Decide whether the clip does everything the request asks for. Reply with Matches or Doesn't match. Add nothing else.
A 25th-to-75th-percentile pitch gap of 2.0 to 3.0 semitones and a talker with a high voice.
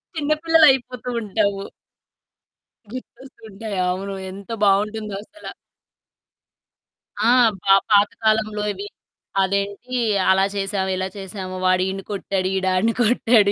Matches